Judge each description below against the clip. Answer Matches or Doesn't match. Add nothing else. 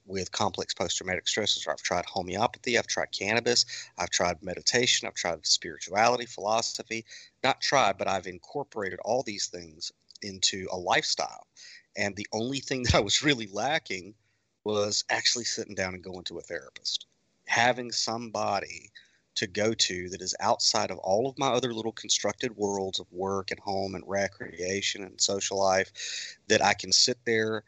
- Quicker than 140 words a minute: Matches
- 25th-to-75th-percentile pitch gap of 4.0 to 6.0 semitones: Doesn't match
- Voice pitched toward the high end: Doesn't match